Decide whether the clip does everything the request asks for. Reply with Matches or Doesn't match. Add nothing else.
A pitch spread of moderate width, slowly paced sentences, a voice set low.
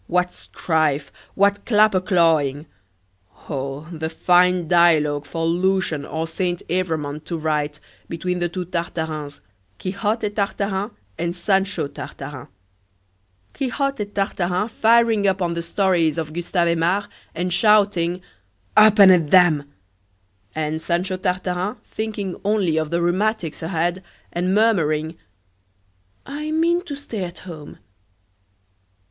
Doesn't match